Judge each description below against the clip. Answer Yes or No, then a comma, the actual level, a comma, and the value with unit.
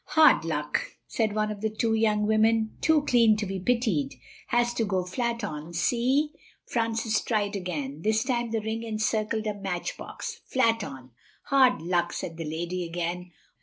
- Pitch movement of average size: Yes, average, 4.4 semitones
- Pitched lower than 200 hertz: No, high, 215 Hz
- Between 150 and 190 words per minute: Yes, average, 165 wpm